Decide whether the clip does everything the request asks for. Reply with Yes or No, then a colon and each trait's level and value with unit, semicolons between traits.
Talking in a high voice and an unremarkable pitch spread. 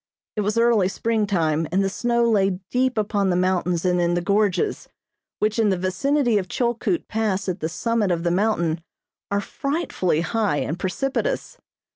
Yes: high, 200 Hz; average, 4.3 semitones